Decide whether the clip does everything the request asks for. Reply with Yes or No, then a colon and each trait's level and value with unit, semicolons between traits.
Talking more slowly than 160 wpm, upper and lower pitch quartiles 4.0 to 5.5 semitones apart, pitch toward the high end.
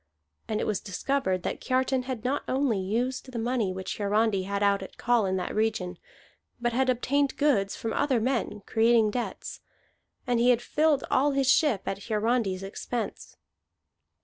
No: average, 170 wpm; average, 4.3 semitones; high, 235 Hz